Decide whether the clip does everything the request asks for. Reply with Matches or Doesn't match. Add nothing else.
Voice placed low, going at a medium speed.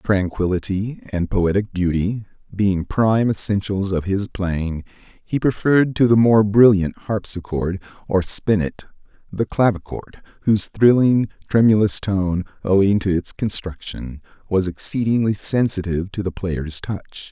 Doesn't match